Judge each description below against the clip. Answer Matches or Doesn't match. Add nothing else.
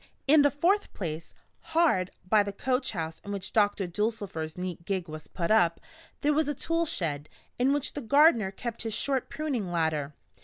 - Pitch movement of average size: Doesn't match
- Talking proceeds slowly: Doesn't match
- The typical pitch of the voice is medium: Doesn't match